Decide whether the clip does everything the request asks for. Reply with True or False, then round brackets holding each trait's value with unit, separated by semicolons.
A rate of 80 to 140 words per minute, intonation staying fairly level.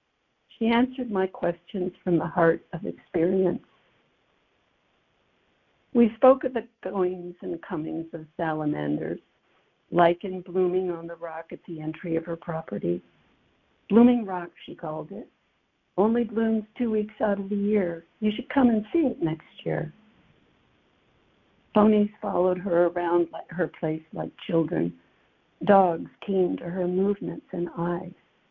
False (135 wpm; 3.9 semitones)